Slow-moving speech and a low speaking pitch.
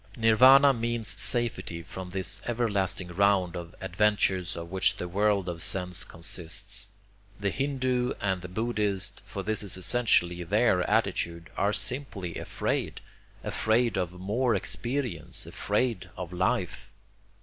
Yes: slow, 125 wpm; low, 100 Hz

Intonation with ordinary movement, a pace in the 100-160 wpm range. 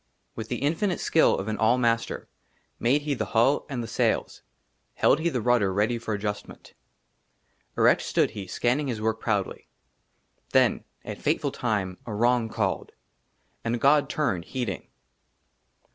Yes: average, 3.4 semitones; average, 150 wpm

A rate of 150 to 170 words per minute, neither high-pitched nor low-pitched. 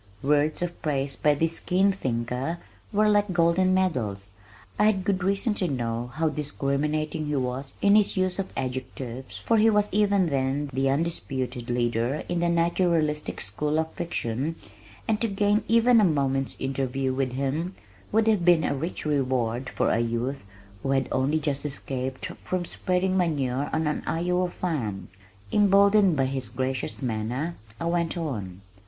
Yes: average, 160 wpm; medium, 150 Hz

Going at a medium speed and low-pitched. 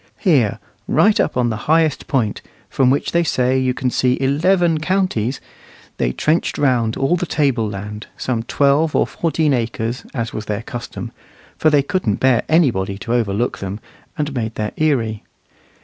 Yes: average, 165 wpm; low, 130 Hz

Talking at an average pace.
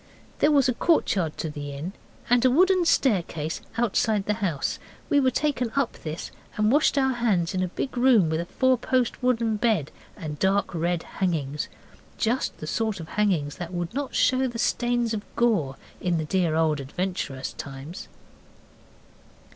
Yes: average, 170 wpm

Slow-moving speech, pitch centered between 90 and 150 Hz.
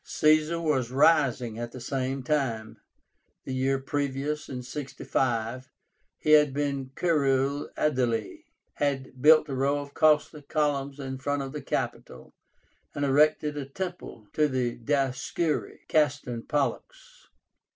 Yes: slow, 130 wpm; medium, 140 Hz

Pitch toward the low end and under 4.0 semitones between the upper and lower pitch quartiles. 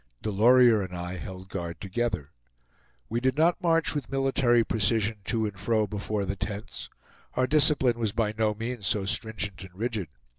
Yes: low, 110 Hz; average, 3.6 semitones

